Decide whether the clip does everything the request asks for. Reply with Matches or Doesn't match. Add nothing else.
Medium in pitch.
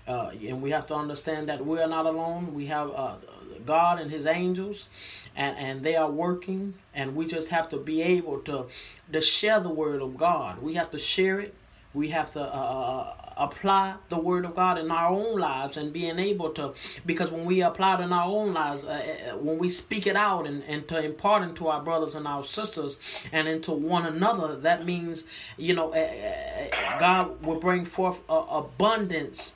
Matches